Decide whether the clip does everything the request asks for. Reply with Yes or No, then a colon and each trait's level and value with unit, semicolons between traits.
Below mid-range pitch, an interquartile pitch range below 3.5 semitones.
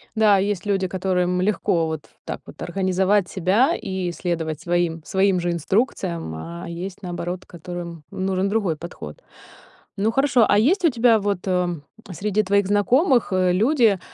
No: high, 190 Hz; average, 2.9 semitones